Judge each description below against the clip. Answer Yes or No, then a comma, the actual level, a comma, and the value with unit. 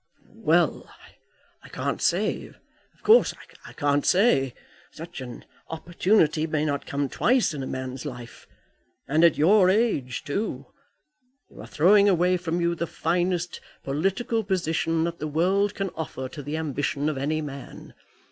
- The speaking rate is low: No, average, 150 wpm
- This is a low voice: No, medium, 160 Hz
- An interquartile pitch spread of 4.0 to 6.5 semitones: Yes, average, 4.3 semitones